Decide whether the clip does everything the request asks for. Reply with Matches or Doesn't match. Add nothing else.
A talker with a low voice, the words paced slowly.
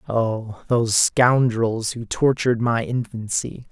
Matches